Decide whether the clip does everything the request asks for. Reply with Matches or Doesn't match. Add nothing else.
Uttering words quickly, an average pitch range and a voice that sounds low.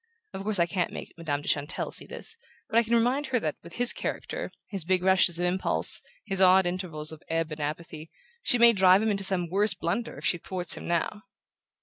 Doesn't match